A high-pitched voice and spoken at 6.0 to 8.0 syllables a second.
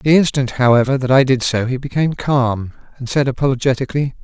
No: low, 130 Hz; 6.3 syllables/s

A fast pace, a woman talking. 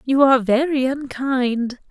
No: slow, 125 wpm; female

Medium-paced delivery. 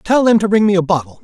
No: fast, 340 wpm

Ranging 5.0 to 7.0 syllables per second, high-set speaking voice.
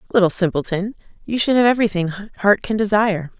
Yes: 6.0 syllables/s; high, 200 Hz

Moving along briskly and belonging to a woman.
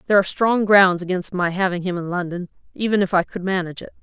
Yes: fast, 240 wpm; female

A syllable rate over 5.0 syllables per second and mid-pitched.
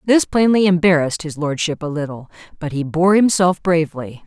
Yes: 5.6 syllables/s; medium, 170 Hz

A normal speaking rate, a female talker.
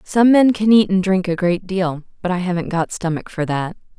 No: fast, 240 wpm; female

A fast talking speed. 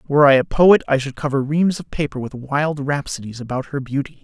Yes: fast, 225 wpm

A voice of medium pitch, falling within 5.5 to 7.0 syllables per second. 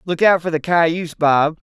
No: medium, 165 Hz; 4.6 syllables/s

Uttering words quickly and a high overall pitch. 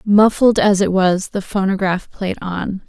No: average, 165 wpm; high, 195 Hz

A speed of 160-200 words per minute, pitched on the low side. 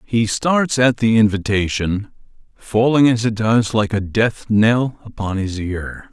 No: average, 145 wpm; low, 110 Hz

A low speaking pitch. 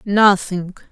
No: high, 195 Hz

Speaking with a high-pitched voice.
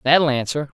No: medium, 140 Hz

